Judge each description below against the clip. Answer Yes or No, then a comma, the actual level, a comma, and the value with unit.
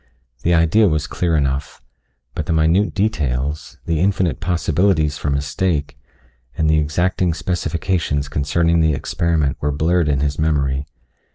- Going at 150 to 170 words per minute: No, slow, 135 wpm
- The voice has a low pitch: Yes, very low, 80 Hz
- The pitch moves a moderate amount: Yes, average, 3.1 semitones